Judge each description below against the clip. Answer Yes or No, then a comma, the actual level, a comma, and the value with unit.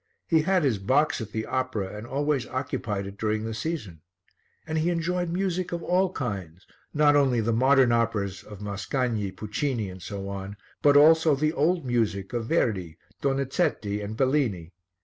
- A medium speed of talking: Yes, average, 170 wpm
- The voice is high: No, low, 120 Hz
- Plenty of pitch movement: Yes, wide, 6.5 semitones